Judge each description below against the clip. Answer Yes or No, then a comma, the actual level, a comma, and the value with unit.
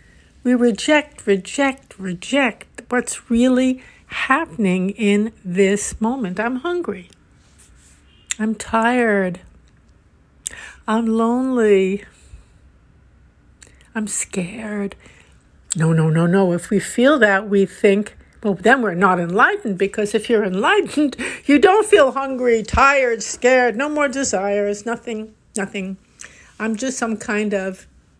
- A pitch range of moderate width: Yes, average, 4.2 semitones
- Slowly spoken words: Yes, slow, 115 wpm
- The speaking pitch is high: Yes, high, 215 Hz